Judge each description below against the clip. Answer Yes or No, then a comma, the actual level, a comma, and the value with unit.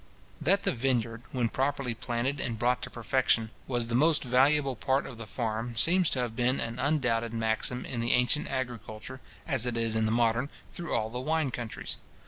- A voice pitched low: Yes, low, 125 Hz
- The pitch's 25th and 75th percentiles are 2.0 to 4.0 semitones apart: Yes, narrow, 2.6 semitones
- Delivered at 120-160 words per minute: No, average, 195 wpm